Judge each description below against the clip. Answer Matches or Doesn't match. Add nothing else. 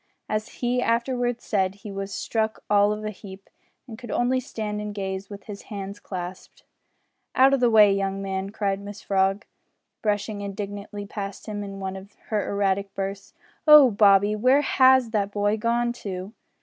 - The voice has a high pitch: Matches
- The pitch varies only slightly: Matches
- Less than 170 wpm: Doesn't match